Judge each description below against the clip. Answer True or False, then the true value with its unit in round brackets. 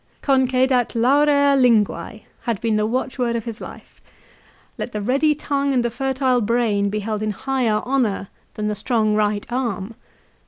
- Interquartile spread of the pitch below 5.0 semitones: True (3.7 semitones)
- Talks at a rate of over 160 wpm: True (180 wpm)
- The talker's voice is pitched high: True (235 Hz)